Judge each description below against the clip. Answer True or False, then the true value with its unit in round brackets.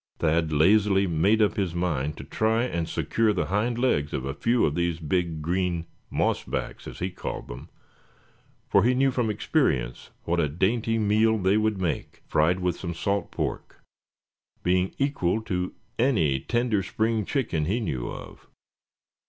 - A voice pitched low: True (95 Hz)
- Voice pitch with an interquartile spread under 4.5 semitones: False (4.8 semitones)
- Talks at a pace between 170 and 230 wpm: False (160 wpm)